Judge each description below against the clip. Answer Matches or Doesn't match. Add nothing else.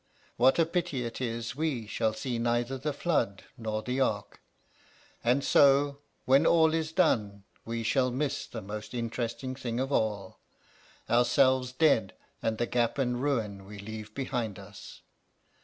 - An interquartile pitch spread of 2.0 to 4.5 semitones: Matches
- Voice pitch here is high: Doesn't match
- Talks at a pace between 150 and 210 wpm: Matches